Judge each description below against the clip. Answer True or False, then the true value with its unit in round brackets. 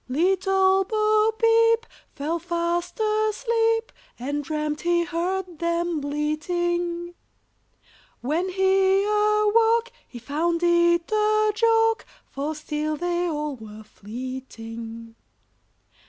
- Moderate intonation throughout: False (5.9 semitones)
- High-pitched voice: True (345 Hz)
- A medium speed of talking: False (95 wpm)